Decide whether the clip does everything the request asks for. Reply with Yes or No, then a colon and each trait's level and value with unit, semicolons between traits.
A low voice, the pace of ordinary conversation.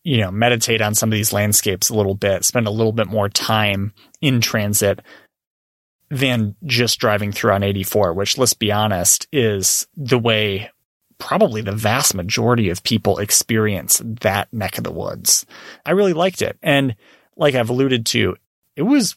Yes: low, 110 Hz; average, 170 wpm